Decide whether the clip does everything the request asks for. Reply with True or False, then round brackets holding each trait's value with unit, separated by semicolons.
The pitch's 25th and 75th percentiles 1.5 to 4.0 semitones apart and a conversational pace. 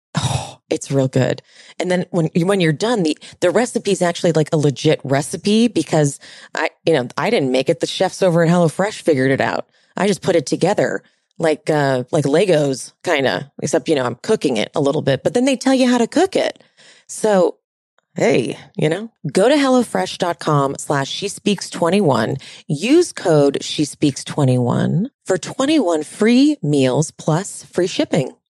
False (5.3 semitones; 180 wpm)